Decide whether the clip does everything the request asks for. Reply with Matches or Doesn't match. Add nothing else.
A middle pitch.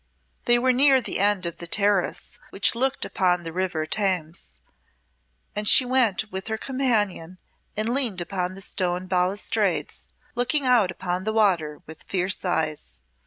Doesn't match